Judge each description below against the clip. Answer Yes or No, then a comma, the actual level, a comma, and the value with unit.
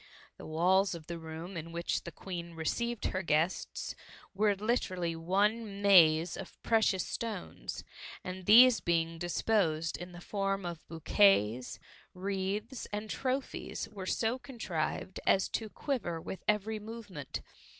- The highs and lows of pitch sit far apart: No, average, 4.0 semitones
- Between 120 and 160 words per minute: Yes, slow, 135 wpm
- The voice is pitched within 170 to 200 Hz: Yes, high, 190 Hz